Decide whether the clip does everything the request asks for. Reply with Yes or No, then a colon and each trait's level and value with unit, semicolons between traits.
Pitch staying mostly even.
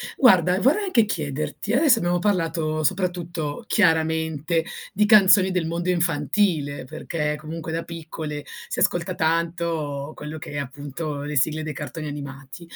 No: average, 3.3 semitones